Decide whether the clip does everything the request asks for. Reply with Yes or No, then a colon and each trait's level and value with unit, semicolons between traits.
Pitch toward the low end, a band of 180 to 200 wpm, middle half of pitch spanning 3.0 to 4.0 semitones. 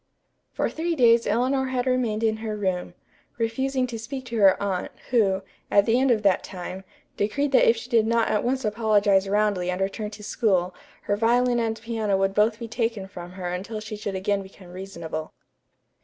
No: high, 215 Hz; average, 195 wpm; average, 3.3 semitones